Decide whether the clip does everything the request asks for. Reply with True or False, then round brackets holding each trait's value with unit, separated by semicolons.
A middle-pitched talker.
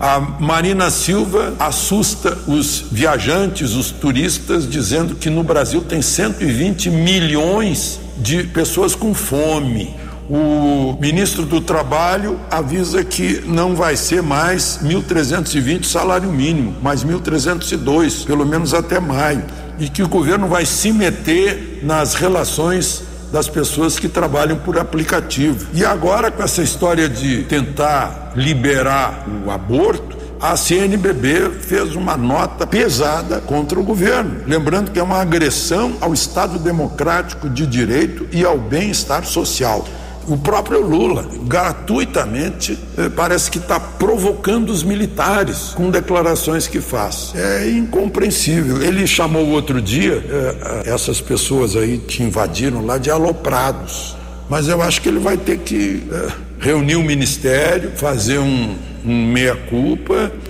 True (160 Hz)